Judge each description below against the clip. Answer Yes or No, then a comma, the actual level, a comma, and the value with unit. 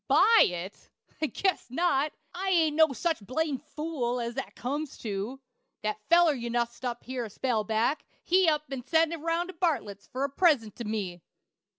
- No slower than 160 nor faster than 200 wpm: Yes, average, 190 wpm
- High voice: Yes, very high, 270 Hz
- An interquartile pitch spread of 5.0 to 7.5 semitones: Yes, wide, 5.6 semitones